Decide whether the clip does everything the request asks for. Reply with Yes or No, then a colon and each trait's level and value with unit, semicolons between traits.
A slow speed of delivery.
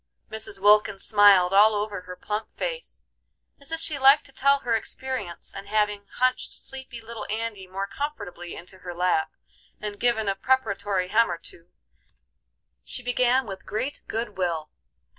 No: average, 160 wpm